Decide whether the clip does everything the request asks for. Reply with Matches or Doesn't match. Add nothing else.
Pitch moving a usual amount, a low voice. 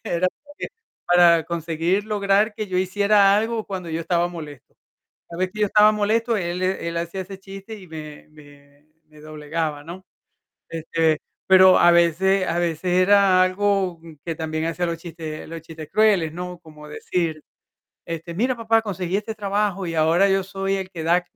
Doesn't match